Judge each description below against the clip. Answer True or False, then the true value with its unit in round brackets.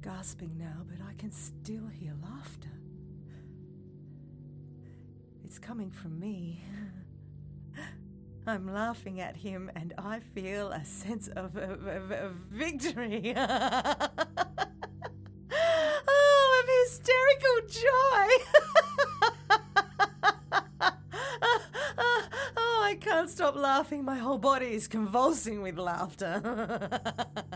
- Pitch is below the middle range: False (225 Hz)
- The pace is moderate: False (90 wpm)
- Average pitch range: False (8.8 semitones)